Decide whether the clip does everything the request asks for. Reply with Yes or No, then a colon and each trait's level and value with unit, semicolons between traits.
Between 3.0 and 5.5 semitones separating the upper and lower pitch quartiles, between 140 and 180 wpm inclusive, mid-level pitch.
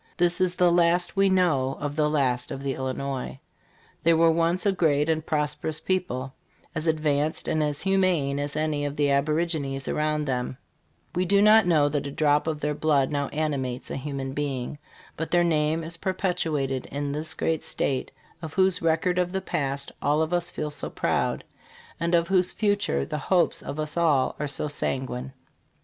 No: average, 3.4 semitones; average, 190 wpm; medium, 150 Hz